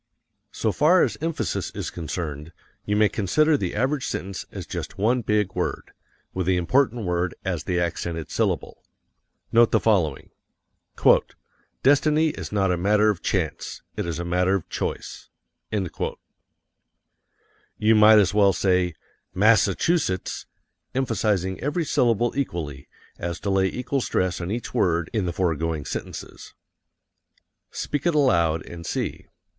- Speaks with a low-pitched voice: Yes, very low, 95 Hz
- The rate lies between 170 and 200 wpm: No, average, 145 wpm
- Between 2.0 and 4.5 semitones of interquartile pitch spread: No, wide, 5.4 semitones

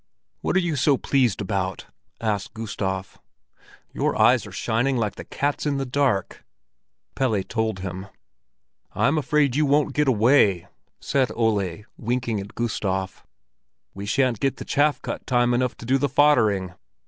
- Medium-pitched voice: No, low, 120 Hz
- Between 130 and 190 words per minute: Yes, average, 155 wpm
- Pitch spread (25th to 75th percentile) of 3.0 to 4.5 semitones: No, wide, 5.4 semitones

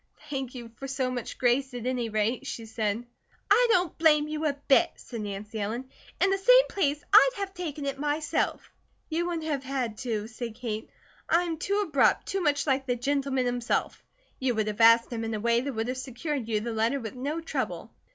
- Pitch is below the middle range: No, very high, 260 Hz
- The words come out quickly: Yes, fast, 210 wpm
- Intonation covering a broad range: No, average, 4.6 semitones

